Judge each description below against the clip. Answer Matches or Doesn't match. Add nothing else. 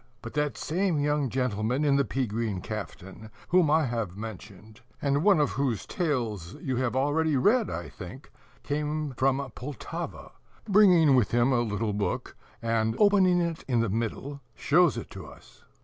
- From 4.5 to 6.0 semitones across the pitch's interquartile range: Matches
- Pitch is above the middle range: Doesn't match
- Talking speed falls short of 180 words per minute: Matches